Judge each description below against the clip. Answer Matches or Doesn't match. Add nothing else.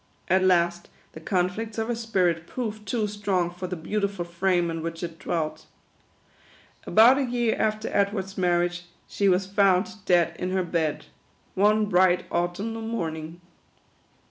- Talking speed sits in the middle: Matches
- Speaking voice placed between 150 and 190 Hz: Matches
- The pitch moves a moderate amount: Matches